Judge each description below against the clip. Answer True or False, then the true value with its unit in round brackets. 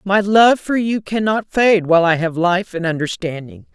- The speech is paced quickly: False (190 wpm)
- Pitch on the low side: False (185 Hz)